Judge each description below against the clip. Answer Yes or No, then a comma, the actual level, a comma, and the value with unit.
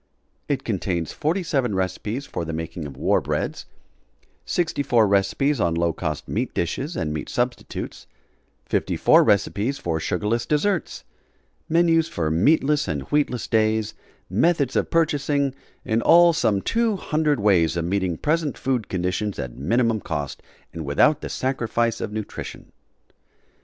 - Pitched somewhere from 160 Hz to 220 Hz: No, low, 110 Hz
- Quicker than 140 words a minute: No, slow, 135 wpm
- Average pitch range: No, wide, 8.7 semitones